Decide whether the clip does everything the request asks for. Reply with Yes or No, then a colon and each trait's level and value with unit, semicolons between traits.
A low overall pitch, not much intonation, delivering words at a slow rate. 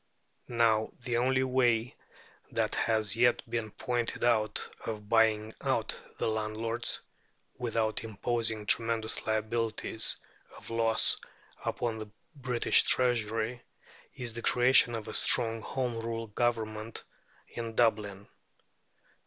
Yes: low, 115 Hz; narrow, 1.6 semitones; slow, 110 wpm